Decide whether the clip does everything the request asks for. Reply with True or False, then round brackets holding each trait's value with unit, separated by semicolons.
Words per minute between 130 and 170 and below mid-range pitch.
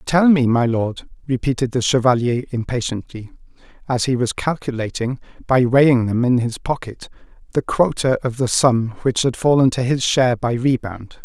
True (165 wpm; 125 Hz)